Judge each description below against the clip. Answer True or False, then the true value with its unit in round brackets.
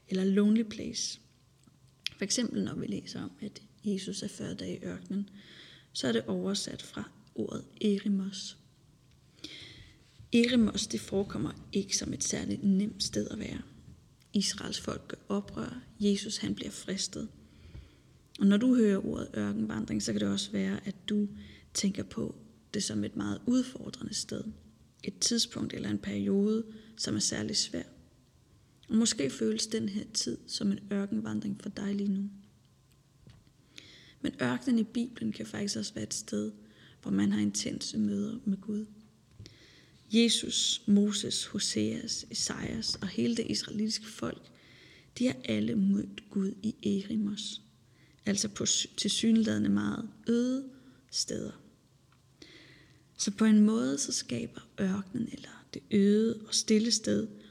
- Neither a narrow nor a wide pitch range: False (8.8 semitones)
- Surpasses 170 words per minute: False (145 wpm)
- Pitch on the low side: False (200 Hz)